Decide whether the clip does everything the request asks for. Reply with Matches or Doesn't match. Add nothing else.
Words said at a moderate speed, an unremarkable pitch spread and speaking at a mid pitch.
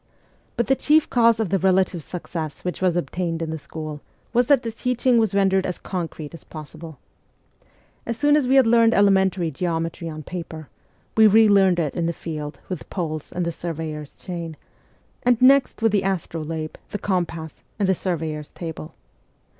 Matches